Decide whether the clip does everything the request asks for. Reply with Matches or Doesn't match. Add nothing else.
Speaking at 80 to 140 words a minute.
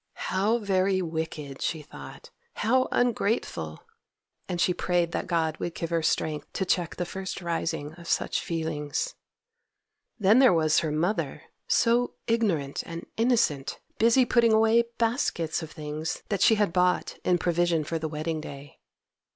Doesn't match